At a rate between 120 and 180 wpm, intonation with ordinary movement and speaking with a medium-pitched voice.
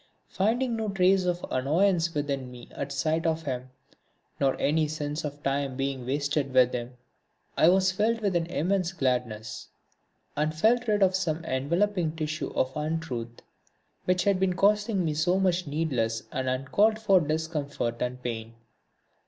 No: average, 160 wpm; wide, 5.7 semitones; medium, 155 Hz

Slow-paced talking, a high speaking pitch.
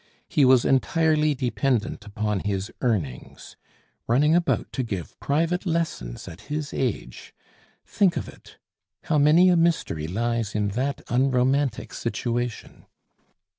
No: slow, 125 wpm; low, 130 Hz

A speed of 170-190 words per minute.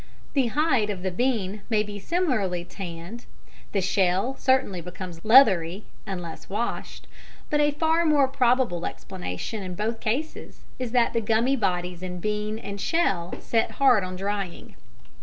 No: average, 150 wpm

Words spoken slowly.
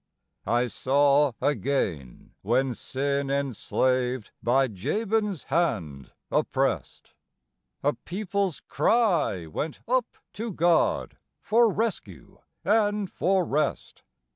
Yes: slow, 90 wpm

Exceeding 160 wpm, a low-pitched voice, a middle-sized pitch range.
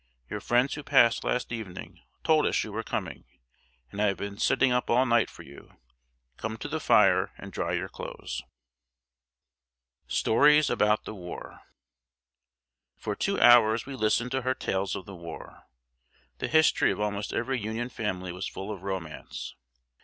Yes: average, 170 wpm; low, 110 Hz; average, 4.1 semitones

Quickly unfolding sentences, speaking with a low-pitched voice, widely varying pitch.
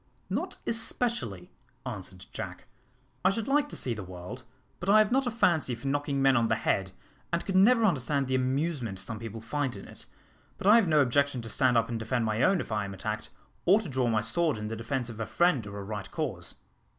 Yes: fast, 230 wpm; low, 130 Hz; wide, 7.5 semitones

